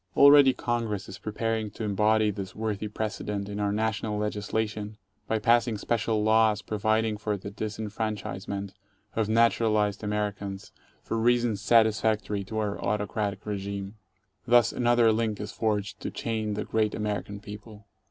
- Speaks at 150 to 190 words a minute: No, average, 140 wpm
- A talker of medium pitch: No, low, 105 Hz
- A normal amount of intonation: No, narrow, 1.3 semitones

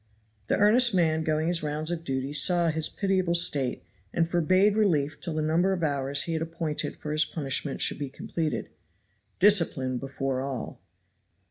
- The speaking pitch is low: No, medium, 160 Hz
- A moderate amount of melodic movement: Yes, average, 3.6 semitones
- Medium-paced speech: Yes, average, 165 wpm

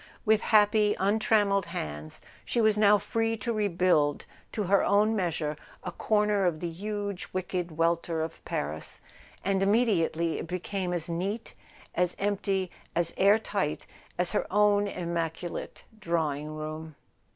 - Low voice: No, medium, 185 Hz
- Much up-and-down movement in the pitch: No, average, 3.8 semitones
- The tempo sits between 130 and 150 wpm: Yes, average, 140 wpm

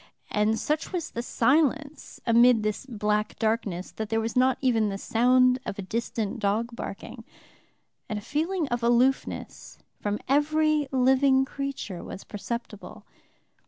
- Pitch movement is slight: No, average, 3.9 semitones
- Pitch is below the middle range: No, high, 240 Hz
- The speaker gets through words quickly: No, average, 140 wpm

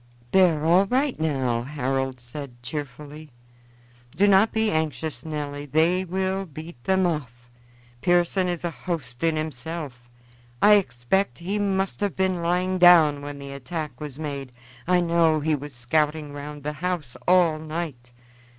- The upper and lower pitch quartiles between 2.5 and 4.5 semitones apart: Yes, average, 4.1 semitones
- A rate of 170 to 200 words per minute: No, average, 150 wpm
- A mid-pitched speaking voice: Yes, medium, 155 Hz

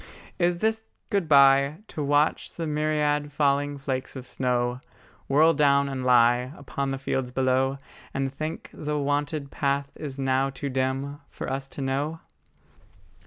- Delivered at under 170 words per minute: Yes, average, 150 wpm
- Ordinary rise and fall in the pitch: No, narrow, 1.9 semitones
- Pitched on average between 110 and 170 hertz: Yes, medium, 140 Hz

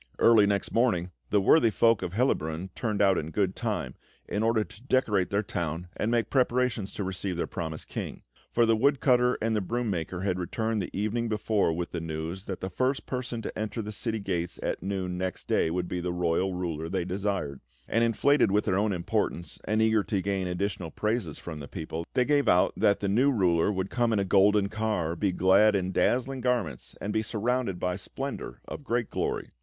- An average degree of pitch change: Yes, average, 4.1 semitones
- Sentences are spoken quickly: Yes, fast, 210 wpm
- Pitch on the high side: No, low, 100 Hz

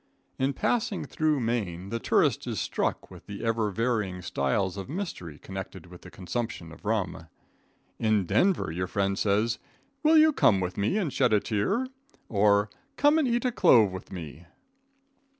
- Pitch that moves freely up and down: Yes, wide, 6.1 semitones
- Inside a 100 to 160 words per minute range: No, average, 170 wpm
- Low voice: Yes, low, 105 Hz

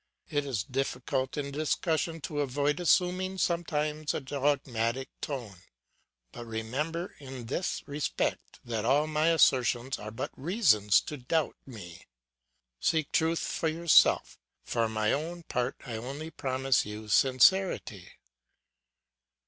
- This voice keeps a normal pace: No, slow, 125 wpm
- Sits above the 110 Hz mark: Yes, medium, 140 Hz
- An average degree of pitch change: Yes, average, 4.9 semitones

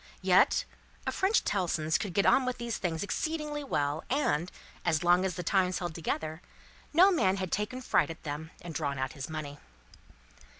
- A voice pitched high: No, medium, 180 Hz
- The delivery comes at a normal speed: Yes, average, 180 wpm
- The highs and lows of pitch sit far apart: Yes, wide, 7.1 semitones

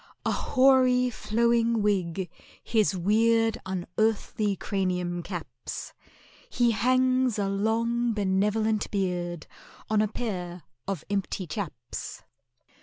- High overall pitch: Yes, high, 210 Hz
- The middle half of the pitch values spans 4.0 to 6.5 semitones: No, average, 3.6 semitones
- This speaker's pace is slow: Yes, slow, 100 wpm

